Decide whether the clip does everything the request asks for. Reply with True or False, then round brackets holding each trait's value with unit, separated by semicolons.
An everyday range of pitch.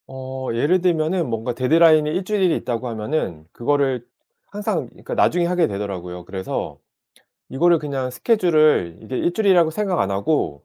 False (6.9 semitones)